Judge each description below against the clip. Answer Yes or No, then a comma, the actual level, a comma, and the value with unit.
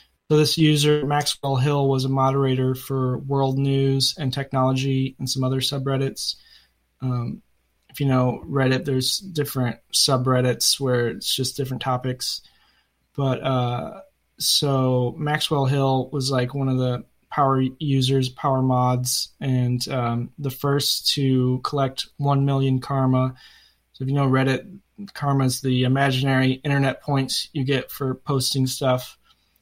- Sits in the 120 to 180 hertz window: Yes, low, 135 Hz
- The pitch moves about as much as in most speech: No, narrow, 1.4 semitones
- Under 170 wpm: Yes, average, 140 wpm